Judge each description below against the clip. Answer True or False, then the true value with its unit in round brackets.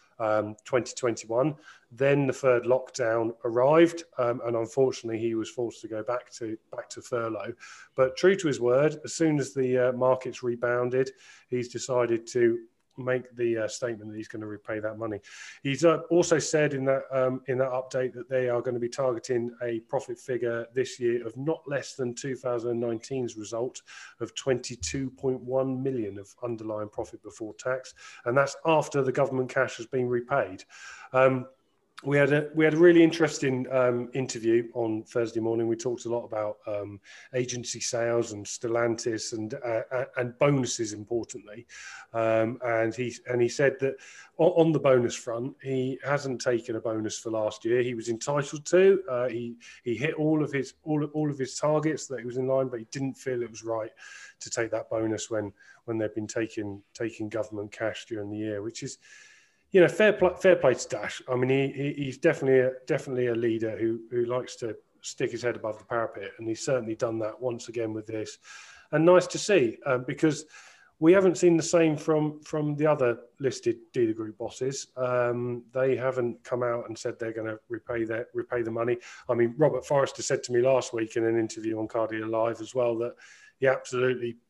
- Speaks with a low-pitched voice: True (125 Hz)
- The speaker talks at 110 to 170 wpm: False (195 wpm)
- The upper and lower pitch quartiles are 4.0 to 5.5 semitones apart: False (3.1 semitones)